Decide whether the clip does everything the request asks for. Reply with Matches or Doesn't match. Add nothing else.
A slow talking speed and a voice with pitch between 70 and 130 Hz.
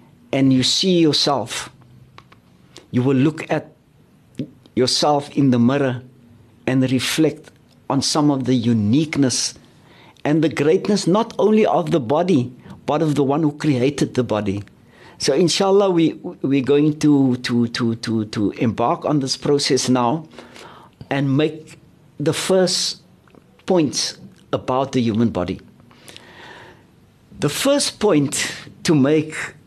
Doesn't match